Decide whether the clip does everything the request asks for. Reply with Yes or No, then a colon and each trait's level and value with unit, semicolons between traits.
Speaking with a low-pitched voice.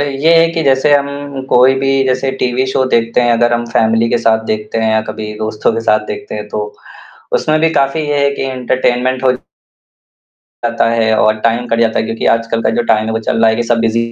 Yes: low, 120 Hz